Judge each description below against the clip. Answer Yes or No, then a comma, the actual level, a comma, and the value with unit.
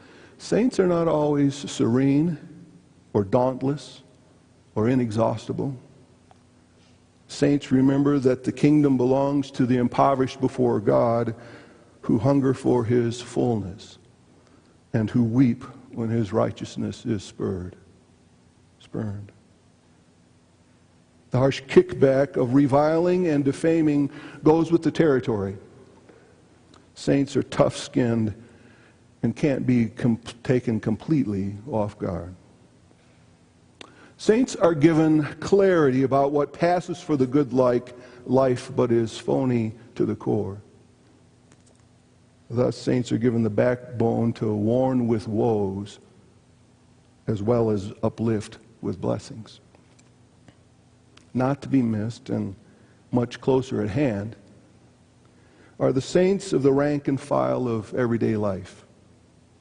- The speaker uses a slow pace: Yes, slow, 110 wpm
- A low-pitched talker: Yes, low, 125 Hz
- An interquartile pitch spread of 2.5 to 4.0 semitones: Yes, average, 3.7 semitones